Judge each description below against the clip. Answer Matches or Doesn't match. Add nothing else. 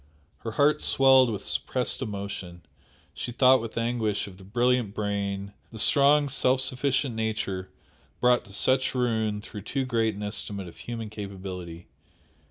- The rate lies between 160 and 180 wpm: Doesn't match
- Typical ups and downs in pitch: Matches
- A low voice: Matches